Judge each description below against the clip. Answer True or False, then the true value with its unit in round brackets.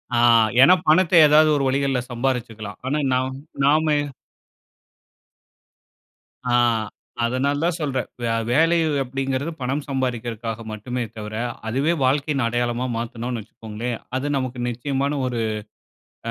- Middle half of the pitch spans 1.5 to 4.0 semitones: True (2.9 semitones)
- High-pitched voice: False (130 Hz)